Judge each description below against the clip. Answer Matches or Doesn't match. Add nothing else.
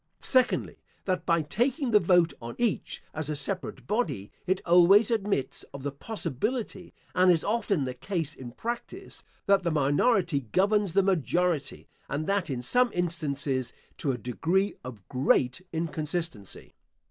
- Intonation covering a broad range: Matches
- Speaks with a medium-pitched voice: Matches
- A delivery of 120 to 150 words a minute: Matches